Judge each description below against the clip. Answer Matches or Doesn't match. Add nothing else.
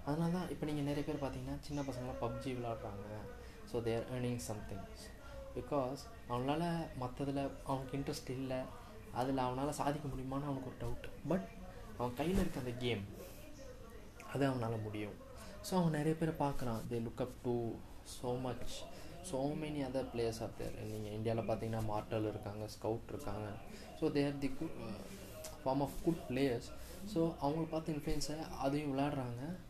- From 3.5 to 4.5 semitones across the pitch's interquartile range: Matches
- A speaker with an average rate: Doesn't match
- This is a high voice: Doesn't match